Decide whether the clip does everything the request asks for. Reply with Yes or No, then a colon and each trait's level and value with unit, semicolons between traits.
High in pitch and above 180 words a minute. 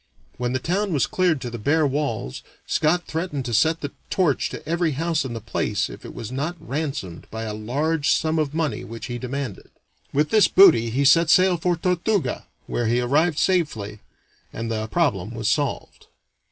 No: medium, 145 Hz; average, 190 wpm